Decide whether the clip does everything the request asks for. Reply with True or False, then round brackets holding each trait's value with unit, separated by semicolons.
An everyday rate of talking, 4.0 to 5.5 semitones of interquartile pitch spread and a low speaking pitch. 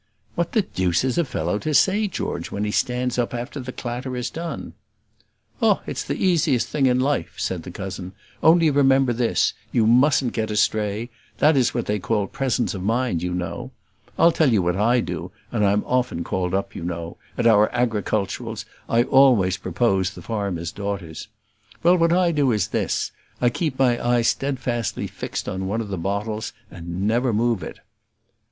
True (185 wpm; 4.9 semitones; 115 Hz)